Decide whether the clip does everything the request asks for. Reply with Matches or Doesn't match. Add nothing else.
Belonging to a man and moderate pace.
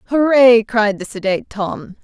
Doesn't match